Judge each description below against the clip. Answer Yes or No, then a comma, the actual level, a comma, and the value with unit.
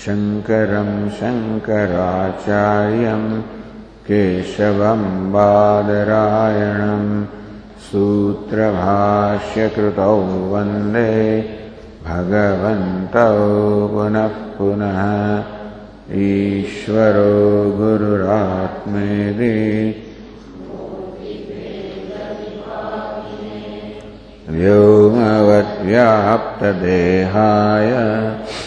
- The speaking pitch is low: Yes, low, 105 Hz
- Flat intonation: Yes, narrow, 0.9 semitones